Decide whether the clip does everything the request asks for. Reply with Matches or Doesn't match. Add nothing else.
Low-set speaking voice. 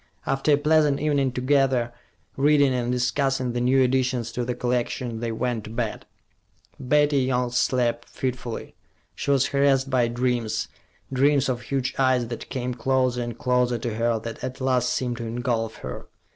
Matches